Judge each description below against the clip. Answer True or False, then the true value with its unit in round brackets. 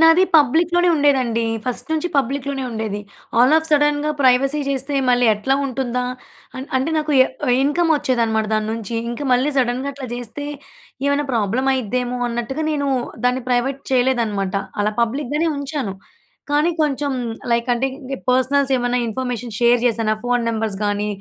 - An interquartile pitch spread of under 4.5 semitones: True (3.3 semitones)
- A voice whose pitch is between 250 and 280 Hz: True (255 Hz)